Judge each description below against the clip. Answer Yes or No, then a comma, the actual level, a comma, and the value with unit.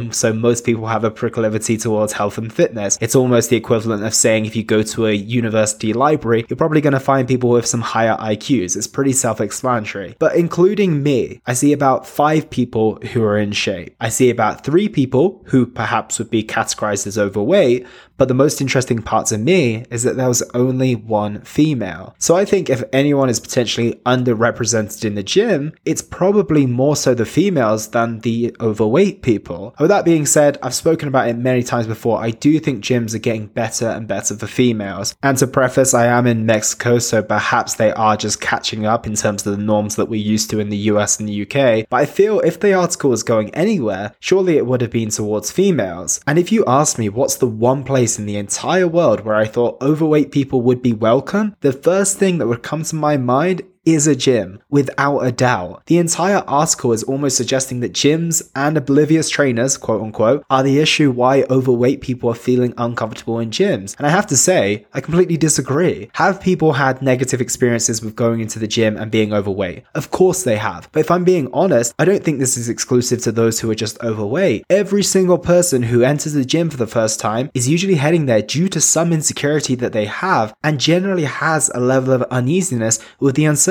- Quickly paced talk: Yes, fast, 215 wpm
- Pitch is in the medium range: No, low, 125 Hz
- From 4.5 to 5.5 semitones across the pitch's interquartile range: Yes, average, 5.0 semitones